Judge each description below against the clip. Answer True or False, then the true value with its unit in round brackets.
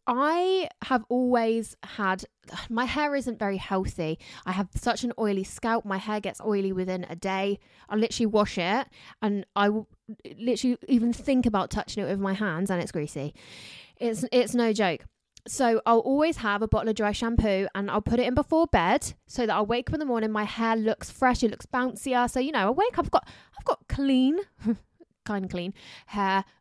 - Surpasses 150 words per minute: True (205 wpm)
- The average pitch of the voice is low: False (225 Hz)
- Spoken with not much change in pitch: False (3.8 semitones)